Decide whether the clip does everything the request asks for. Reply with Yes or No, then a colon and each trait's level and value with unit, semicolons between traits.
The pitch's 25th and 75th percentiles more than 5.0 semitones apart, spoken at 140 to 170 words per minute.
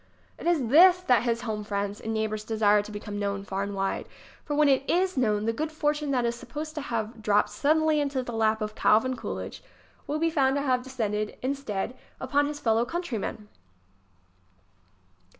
No: wide, 5.4 semitones; average, 190 wpm